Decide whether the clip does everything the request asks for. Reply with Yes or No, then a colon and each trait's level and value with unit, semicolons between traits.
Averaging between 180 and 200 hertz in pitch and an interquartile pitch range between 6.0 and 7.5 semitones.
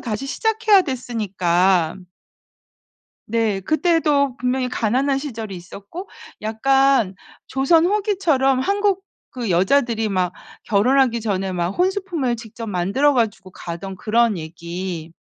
No: high, 235 Hz; wide, 6.5 semitones